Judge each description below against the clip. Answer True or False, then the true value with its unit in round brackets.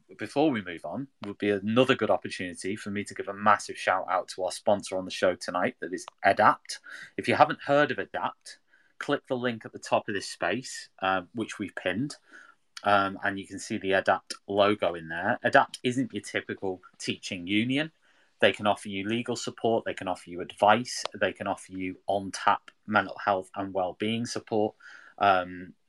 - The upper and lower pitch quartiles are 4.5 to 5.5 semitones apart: False (3.1 semitones)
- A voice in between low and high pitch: False (100 Hz)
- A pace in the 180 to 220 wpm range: True (200 wpm)